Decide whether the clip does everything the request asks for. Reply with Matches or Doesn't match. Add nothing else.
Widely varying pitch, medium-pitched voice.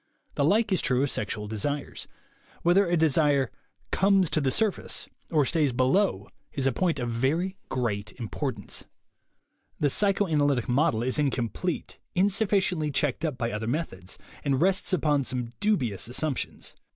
Matches